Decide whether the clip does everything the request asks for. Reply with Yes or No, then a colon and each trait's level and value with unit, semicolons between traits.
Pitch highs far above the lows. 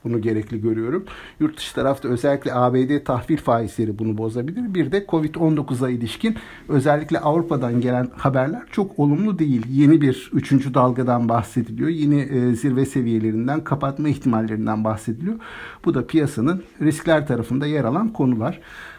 No: average, 4.2 semitones